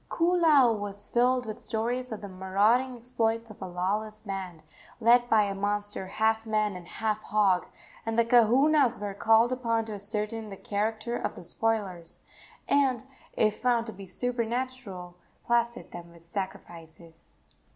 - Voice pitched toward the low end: No, high, 220 Hz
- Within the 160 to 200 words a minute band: No, average, 150 wpm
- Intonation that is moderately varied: Yes, average, 3.3 semitones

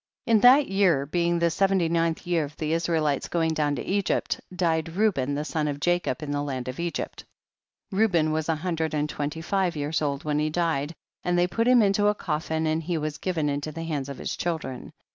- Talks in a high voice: No, medium, 160 Hz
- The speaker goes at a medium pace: No, fast, 220 wpm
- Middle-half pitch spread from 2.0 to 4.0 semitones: Yes, average, 2.8 semitones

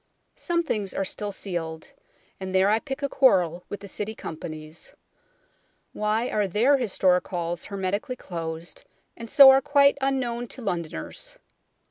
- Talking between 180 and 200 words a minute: No, average, 145 wpm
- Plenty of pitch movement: Yes, wide, 6.2 semitones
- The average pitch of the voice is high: Yes, high, 200 Hz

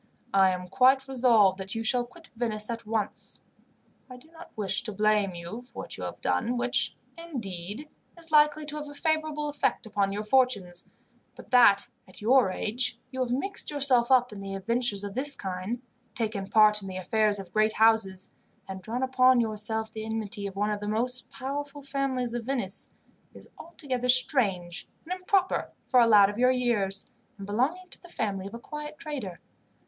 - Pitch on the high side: Yes, high, 230 Hz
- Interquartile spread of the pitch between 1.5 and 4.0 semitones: No, average, 4.5 semitones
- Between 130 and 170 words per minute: No, average, 185 wpm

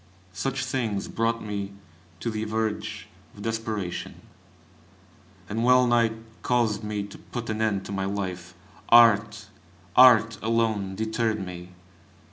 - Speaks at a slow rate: Yes, slow, 120 wpm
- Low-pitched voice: Yes, low, 110 Hz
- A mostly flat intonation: Yes, narrow, 2.3 semitones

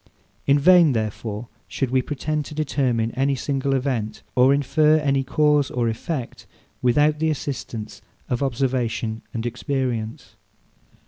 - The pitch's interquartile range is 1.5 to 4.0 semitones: Yes, average, 3.6 semitones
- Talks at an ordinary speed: No, slow, 130 wpm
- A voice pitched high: No, low, 135 Hz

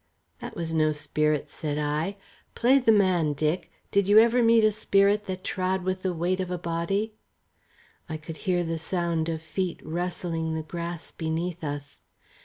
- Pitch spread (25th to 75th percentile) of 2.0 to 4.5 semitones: Yes, average, 3.1 semitones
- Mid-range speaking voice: Yes, medium, 175 Hz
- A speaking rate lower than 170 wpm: No, average, 175 wpm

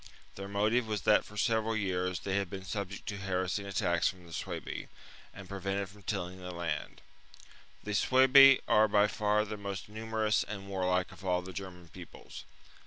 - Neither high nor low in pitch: No, low, 100 Hz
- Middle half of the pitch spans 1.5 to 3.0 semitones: Yes, narrow, 2.5 semitones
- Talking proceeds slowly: No, average, 190 wpm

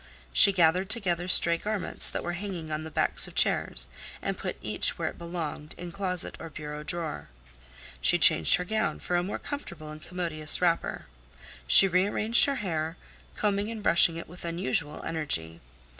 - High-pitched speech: No, medium, 170 Hz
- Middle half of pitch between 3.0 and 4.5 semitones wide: Yes, average, 3.6 semitones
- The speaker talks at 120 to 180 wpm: Yes, average, 175 wpm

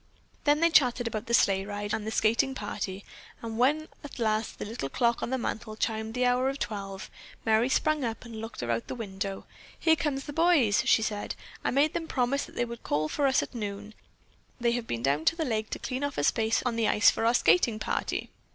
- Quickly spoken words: Yes, fast, 230 wpm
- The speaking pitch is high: Yes, high, 230 Hz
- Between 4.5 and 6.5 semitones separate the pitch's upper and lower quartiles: No, average, 4.0 semitones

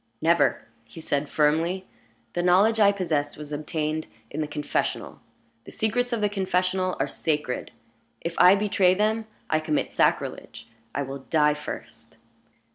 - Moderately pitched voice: Yes, medium, 170 Hz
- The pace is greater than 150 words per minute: No, average, 145 wpm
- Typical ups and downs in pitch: Yes, average, 4.4 semitones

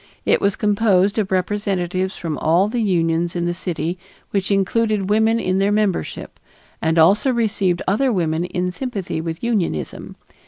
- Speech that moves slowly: No, average, 155 wpm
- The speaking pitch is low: No, high, 190 Hz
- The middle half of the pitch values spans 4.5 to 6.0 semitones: No, average, 3.3 semitones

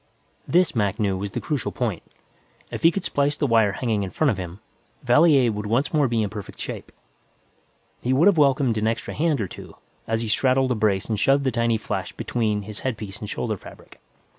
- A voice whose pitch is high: No, low, 115 Hz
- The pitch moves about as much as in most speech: Yes, average, 4.6 semitones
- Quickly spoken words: Yes, fast, 215 wpm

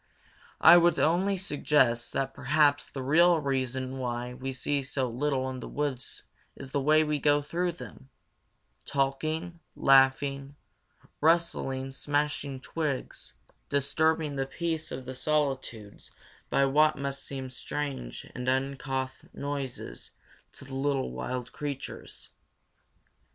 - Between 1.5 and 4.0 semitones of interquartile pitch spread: Yes, narrow, 2.4 semitones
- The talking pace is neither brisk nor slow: No, slow, 125 wpm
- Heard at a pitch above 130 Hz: Yes, medium, 140 Hz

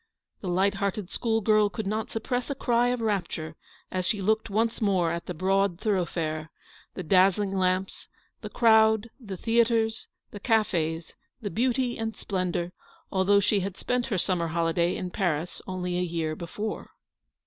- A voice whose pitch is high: Yes, high, 195 Hz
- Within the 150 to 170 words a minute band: Yes, average, 160 wpm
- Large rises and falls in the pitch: No, average, 3.7 semitones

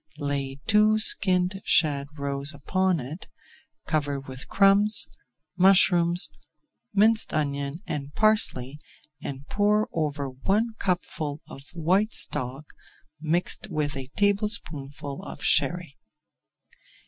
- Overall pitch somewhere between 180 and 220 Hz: No, medium, 155 Hz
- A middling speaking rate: No, slow, 100 wpm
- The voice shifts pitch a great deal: Yes, wide, 5.7 semitones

